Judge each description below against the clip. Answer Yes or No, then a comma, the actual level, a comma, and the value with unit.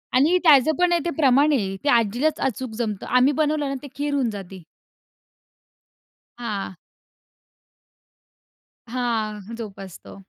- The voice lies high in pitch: Yes, very high, 250 Hz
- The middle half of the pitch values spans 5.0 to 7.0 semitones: Yes, wide, 5.5 semitones